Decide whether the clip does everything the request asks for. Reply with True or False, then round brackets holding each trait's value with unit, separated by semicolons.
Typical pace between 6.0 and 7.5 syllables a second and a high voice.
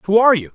False (7.8 syllables/s; 200 Hz)